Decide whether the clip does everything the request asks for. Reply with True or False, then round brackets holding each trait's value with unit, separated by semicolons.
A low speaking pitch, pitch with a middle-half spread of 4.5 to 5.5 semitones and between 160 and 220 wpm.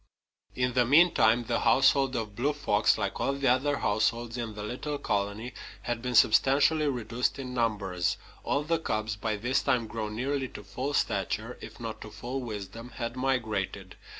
False (120 Hz; 3.8 semitones; 175 wpm)